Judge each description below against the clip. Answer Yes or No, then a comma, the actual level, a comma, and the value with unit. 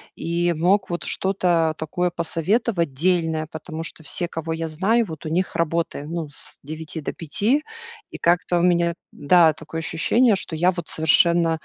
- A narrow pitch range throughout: Yes, narrow, 1.9 semitones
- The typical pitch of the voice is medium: Yes, medium, 170 Hz